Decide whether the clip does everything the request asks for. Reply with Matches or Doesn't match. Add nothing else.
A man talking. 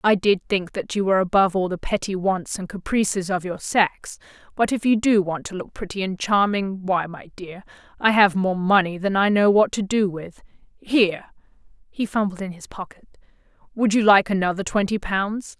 Doesn't match